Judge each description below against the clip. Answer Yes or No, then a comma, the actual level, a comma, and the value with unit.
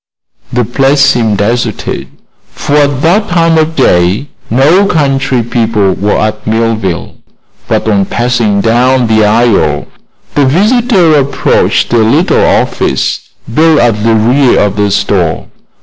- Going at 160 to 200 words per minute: No, slow, 135 wpm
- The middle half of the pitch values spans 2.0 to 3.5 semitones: No, average, 5.0 semitones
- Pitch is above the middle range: No, low, 120 Hz